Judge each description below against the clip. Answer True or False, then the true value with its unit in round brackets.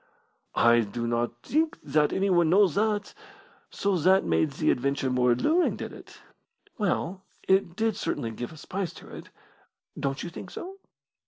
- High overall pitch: False (170 Hz)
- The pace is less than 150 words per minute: False (160 wpm)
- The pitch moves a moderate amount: False (8.4 semitones)